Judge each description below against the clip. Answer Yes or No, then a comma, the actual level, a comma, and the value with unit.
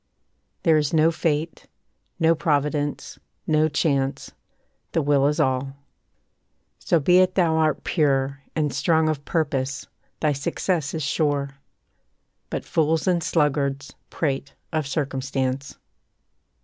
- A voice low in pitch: No, medium, 150 Hz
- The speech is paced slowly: Yes, slow, 120 wpm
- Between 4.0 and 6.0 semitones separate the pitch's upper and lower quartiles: No, narrow, 2.6 semitones